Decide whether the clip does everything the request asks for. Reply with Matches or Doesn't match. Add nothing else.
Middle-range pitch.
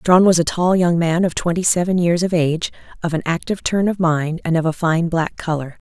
Matches